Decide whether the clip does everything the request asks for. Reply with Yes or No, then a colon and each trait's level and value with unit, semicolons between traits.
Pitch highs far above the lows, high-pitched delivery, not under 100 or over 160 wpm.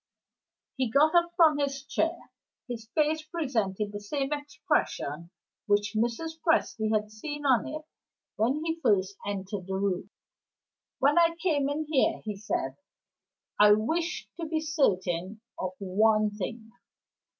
Yes: wide, 7.1 semitones; high, 240 Hz; average, 140 wpm